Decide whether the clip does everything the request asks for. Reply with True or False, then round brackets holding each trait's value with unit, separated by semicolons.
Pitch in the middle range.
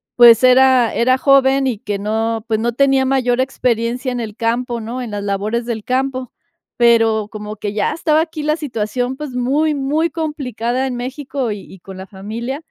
False (245 Hz)